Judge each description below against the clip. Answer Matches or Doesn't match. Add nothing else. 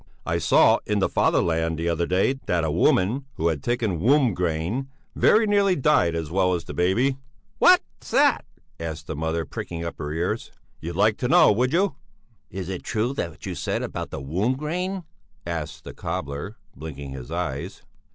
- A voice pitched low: Matches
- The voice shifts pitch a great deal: Matches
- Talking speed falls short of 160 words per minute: Doesn't match